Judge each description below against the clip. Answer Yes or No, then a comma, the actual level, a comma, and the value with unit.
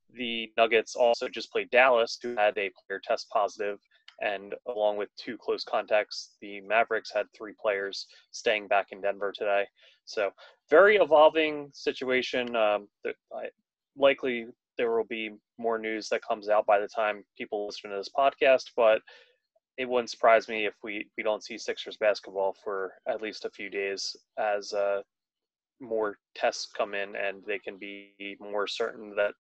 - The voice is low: Yes, low, 110 Hz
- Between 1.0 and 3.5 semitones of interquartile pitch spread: No, average, 4.0 semitones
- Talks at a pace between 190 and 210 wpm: No, average, 165 wpm